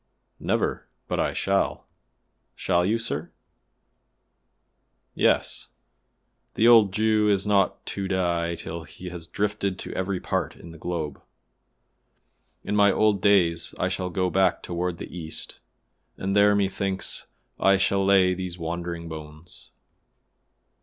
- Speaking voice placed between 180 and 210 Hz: No, very low, 95 Hz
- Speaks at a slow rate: Yes, slow, 130 wpm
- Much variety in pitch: No, average, 2.7 semitones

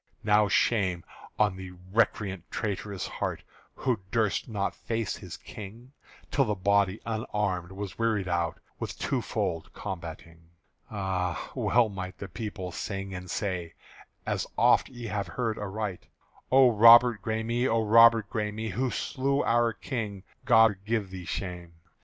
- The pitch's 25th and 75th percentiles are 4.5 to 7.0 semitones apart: No, average, 3.4 semitones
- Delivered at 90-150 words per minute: Yes, average, 140 wpm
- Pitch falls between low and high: No, low, 105 Hz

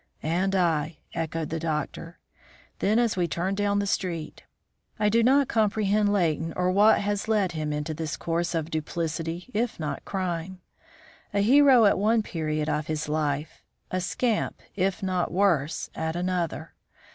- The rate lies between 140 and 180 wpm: Yes, average, 155 wpm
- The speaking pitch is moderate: Yes, medium, 180 Hz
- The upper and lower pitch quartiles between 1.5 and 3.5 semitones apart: No, average, 4.2 semitones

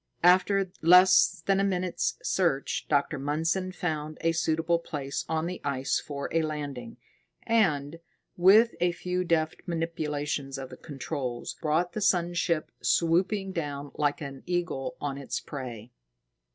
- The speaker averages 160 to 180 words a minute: No, average, 140 wpm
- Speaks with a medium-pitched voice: Yes, medium, 160 Hz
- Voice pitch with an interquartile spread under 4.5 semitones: Yes, average, 3.8 semitones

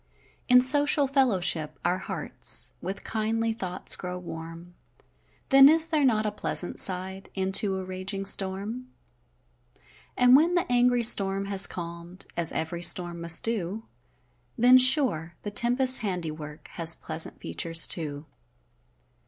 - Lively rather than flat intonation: Yes, wide, 6.2 semitones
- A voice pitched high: Yes, high, 195 Hz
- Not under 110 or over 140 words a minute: Yes, slow, 135 wpm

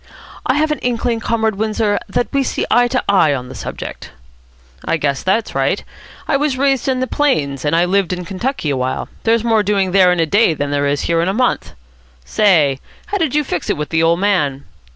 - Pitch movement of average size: No, wide, 7.3 semitones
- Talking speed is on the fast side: Yes, fast, 225 wpm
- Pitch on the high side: Yes, high, 200 Hz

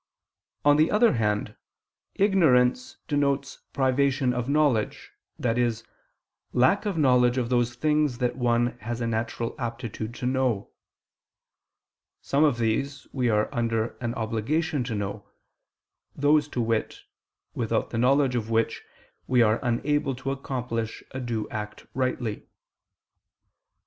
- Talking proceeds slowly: Yes, slow, 130 wpm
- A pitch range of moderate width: Yes, average, 3.2 semitones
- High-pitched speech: No, low, 125 Hz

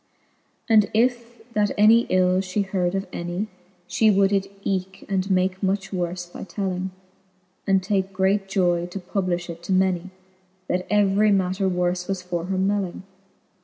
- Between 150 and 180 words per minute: Yes, average, 165 wpm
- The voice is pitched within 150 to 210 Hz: Yes, high, 190 Hz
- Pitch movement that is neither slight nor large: No, narrow, 1.6 semitones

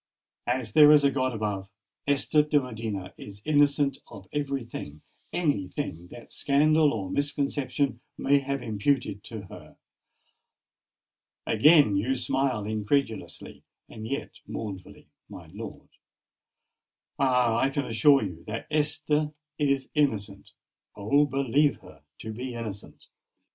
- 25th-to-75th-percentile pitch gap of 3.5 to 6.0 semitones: Yes, average, 5.1 semitones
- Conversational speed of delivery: No, slow, 115 wpm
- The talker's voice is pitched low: Yes, low, 130 Hz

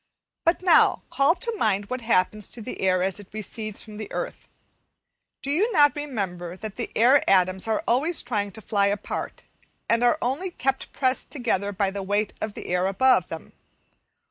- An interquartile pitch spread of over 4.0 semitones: Yes, average, 5.2 semitones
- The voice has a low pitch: No, high, 215 Hz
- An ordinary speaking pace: Yes, average, 180 wpm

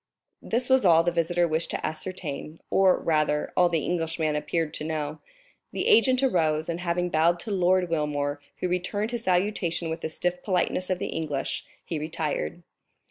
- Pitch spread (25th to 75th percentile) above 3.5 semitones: No, narrow, 2.6 semitones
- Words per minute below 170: No, average, 175 wpm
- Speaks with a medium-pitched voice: Yes, medium, 170 Hz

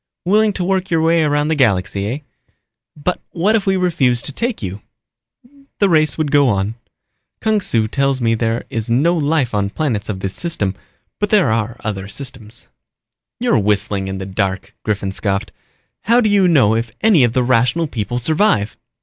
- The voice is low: Yes, low, 125 Hz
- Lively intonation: Yes, wide, 8.1 semitones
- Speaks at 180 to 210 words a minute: Yes, average, 185 wpm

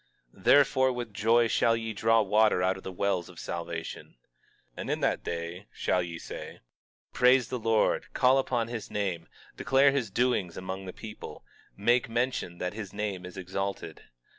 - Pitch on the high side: No, low, 105 Hz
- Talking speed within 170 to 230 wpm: Yes, average, 175 wpm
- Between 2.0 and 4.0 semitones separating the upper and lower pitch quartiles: No, average, 4.4 semitones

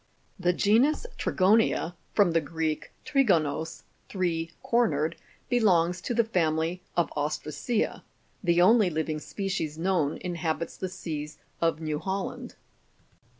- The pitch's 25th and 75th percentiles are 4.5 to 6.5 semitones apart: No, average, 3.6 semitones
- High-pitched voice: No, medium, 175 Hz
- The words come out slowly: Yes, slow, 115 wpm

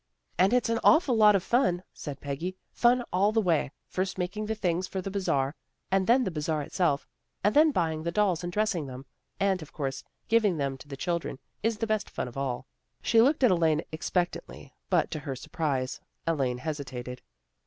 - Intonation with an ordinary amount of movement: No, wide, 6.4 semitones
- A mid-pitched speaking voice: Yes, medium, 175 Hz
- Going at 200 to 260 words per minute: Yes, fast, 205 wpm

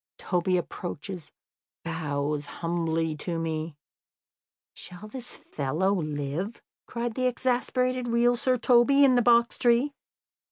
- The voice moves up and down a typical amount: No, wide, 7.0 semitones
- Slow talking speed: Yes, slow, 120 wpm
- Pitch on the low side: No, high, 195 Hz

